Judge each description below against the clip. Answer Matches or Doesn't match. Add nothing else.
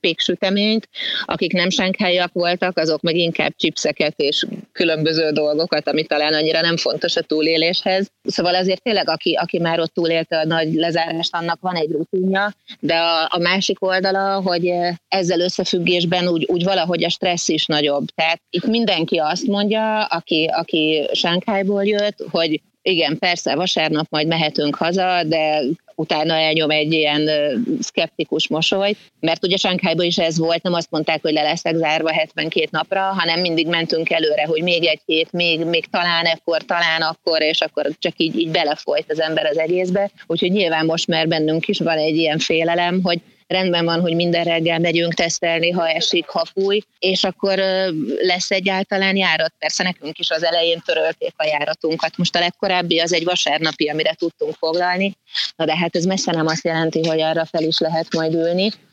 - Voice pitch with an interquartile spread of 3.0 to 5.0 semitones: Doesn't match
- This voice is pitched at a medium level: Matches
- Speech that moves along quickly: Matches